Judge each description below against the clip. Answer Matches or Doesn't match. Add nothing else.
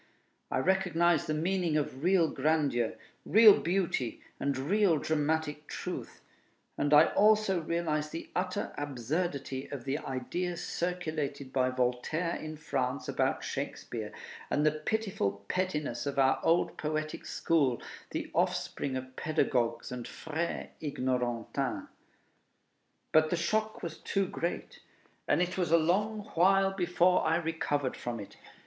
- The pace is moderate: Doesn't match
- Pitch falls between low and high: Matches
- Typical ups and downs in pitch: Matches